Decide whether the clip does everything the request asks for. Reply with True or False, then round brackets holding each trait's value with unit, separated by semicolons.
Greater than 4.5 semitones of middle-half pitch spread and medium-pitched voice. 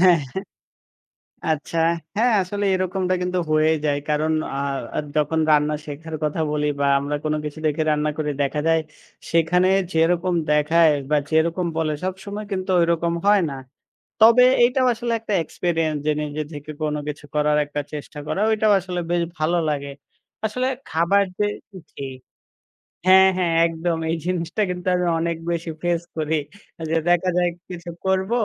False (3.4 semitones; 165 Hz)